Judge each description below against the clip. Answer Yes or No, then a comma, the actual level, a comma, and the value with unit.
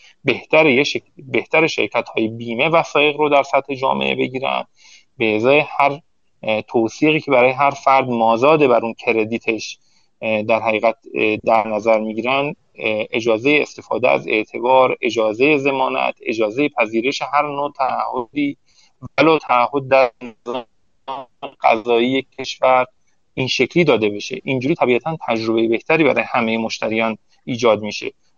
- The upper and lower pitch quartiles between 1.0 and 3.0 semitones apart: No, average, 4.0 semitones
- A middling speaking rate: Yes, average, 120 wpm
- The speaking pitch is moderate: No, low, 125 Hz